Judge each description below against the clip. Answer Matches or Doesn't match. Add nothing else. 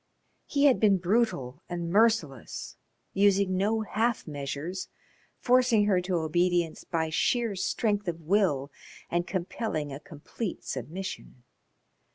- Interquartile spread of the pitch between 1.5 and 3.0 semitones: Doesn't match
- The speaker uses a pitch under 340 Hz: Matches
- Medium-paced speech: Doesn't match